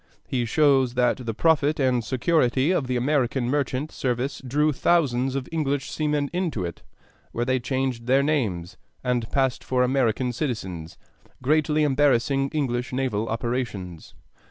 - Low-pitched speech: Yes, low, 130 Hz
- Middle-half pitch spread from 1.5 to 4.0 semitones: Yes, average, 3.0 semitones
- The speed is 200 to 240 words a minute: No, average, 140 wpm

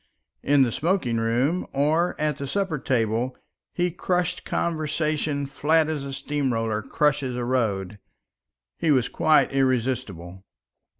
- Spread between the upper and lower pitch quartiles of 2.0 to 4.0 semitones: No, average, 4.5 semitones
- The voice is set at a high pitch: No, medium, 140 Hz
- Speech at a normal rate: No, slow, 130 wpm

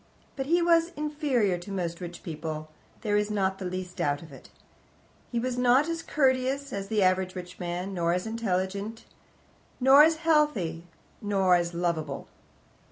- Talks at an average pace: Yes, average, 165 wpm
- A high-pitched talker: Yes, high, 195 Hz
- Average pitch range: No, wide, 6.8 semitones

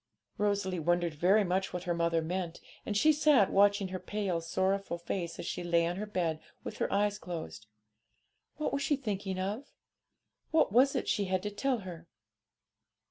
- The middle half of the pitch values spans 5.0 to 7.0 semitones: No, average, 3.2 semitones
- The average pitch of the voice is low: No, high, 190 Hz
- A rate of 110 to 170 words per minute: No, average, 180 wpm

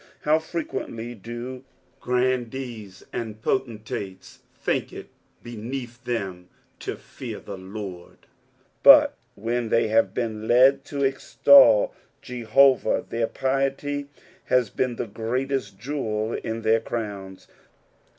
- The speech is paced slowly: Yes, slow, 110 wpm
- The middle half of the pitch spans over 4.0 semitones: No, average, 3.5 semitones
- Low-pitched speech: Yes, low, 120 Hz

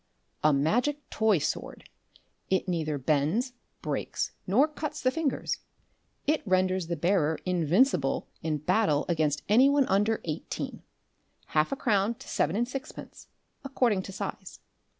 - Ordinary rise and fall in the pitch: No, wide, 8.0 semitones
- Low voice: No, high, 190 Hz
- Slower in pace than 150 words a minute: Yes, slow, 135 wpm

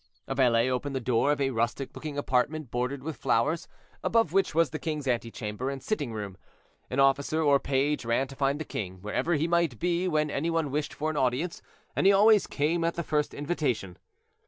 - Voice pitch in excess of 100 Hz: Yes, medium, 140 Hz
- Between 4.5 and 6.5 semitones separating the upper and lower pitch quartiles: No, average, 4.0 semitones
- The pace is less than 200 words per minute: No, fast, 205 wpm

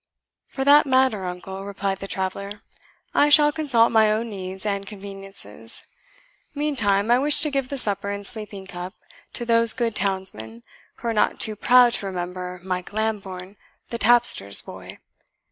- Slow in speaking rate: No, average, 160 wpm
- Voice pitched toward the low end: No, high, 205 Hz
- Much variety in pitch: No, average, 3.9 semitones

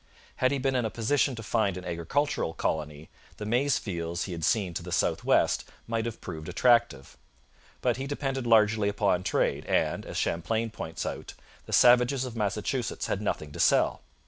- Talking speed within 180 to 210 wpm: Yes, average, 185 wpm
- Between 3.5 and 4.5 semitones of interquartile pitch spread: No, wide, 5.5 semitones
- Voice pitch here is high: No, low, 110 Hz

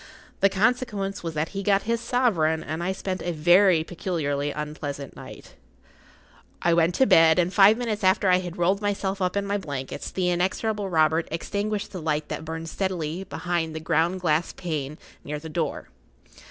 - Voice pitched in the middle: Yes, medium, 175 Hz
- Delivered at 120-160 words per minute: No, average, 180 wpm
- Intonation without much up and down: No, average, 3.7 semitones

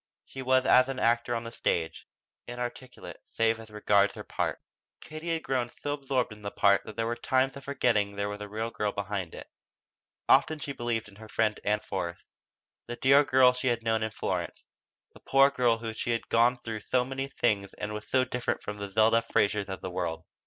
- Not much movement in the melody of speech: No, average, 3.6 semitones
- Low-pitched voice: Yes, low, 115 Hz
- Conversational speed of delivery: No, fast, 215 wpm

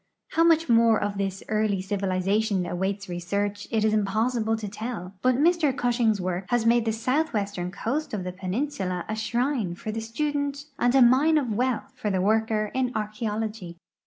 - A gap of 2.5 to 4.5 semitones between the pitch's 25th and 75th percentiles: Yes, average, 3.9 semitones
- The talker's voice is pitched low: No, high, 220 Hz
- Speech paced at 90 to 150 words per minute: No, average, 180 wpm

